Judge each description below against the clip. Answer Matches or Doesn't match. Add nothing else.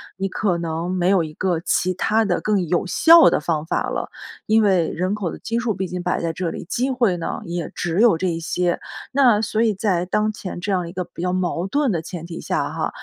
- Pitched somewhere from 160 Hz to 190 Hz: Matches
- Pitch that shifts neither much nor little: Matches